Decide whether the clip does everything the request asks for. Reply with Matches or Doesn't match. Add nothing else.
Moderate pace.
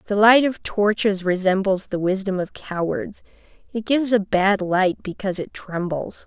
Matches